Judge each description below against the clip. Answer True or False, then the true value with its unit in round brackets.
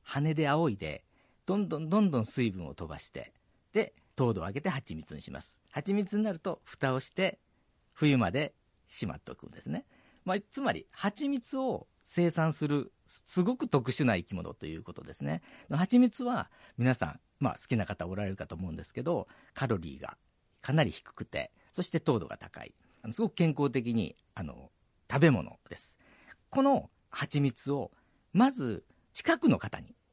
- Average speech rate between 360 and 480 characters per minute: False (315 characters per minute)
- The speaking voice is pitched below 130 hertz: False (140 Hz)